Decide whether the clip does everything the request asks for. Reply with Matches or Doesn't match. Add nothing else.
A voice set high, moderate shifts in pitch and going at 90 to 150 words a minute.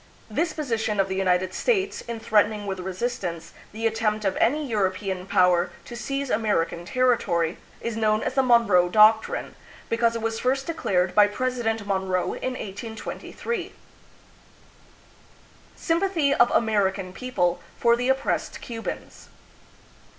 Matches